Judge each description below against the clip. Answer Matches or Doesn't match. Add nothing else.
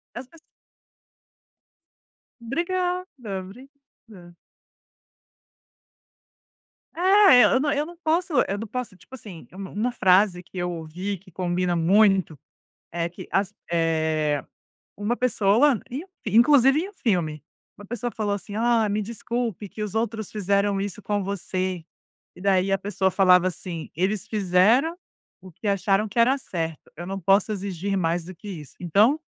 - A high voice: Matches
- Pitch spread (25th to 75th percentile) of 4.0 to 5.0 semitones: Matches